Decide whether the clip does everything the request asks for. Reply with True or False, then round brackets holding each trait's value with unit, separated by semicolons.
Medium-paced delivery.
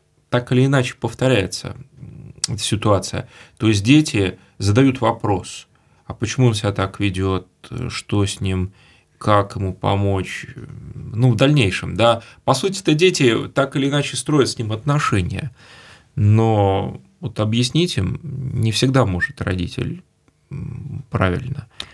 True (130 wpm)